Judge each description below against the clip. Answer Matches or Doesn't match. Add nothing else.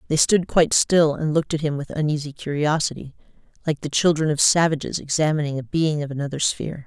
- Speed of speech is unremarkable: Matches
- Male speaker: Doesn't match